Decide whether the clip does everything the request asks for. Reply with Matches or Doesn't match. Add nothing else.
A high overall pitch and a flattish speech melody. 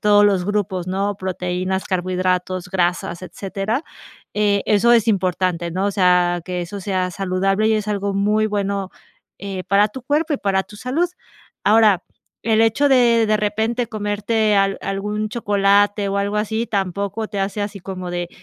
Matches